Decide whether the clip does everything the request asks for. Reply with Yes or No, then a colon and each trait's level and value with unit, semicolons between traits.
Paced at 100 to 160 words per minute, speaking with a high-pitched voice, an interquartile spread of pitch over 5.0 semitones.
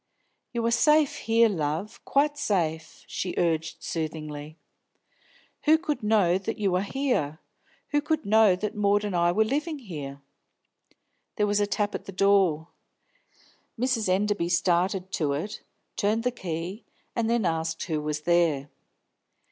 Yes: average, 150 wpm; high, 195 Hz; wide, 5.6 semitones